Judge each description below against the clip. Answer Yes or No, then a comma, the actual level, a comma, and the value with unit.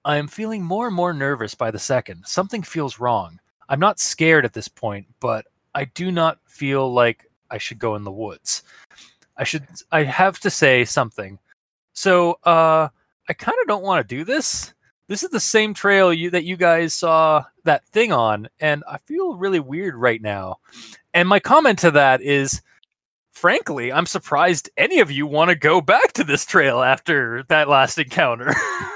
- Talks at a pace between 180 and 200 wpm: Yes, average, 190 wpm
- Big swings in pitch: Yes, wide, 6.1 semitones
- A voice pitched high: No, medium, 155 Hz